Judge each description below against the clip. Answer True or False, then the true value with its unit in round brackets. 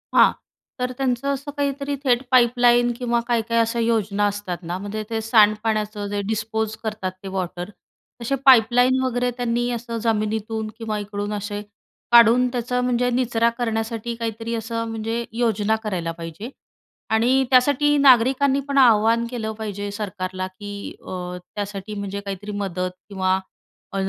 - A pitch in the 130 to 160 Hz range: False (225 Hz)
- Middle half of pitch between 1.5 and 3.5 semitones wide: True (2.9 semitones)